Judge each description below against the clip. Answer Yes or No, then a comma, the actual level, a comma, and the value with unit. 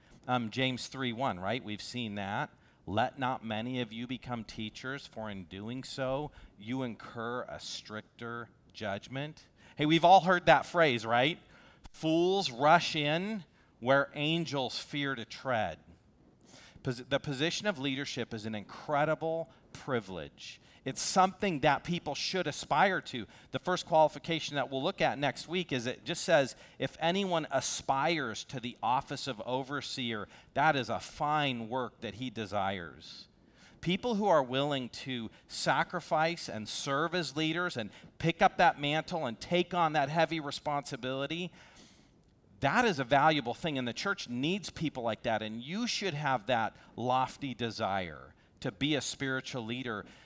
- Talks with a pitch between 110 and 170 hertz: Yes, low, 135 Hz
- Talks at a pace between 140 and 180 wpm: Yes, average, 155 wpm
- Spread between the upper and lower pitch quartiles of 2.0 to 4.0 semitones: No, average, 5.2 semitones